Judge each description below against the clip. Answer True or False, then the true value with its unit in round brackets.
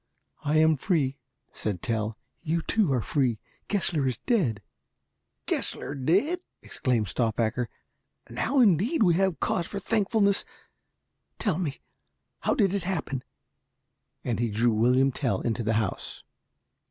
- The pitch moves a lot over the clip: True (8.4 semitones)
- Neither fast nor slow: False (130 wpm)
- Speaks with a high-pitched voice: False (145 Hz)